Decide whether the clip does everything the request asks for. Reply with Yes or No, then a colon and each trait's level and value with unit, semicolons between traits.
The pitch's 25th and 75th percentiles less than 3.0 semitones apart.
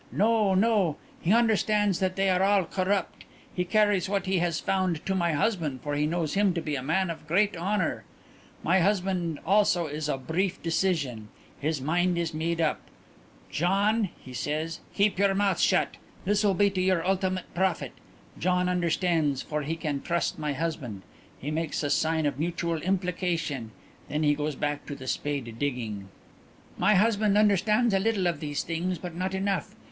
No: average, 4.1 semitones